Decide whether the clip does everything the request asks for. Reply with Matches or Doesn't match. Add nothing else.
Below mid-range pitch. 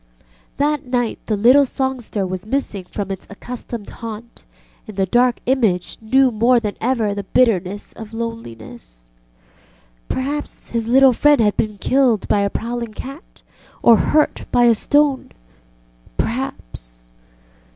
Doesn't match